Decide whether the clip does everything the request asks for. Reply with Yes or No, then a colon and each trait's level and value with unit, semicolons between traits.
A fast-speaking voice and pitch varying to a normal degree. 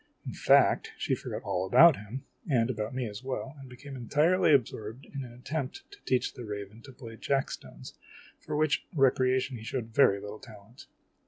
No: average, 185 wpm; average, 3.7 semitones